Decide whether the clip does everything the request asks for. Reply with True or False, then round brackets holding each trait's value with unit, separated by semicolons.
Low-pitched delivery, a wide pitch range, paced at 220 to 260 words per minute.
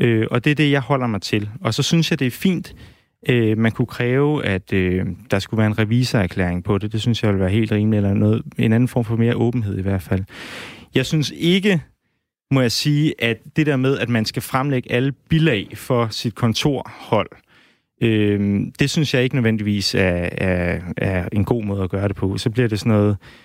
False (115 Hz; 4.5 semitones; 225 wpm)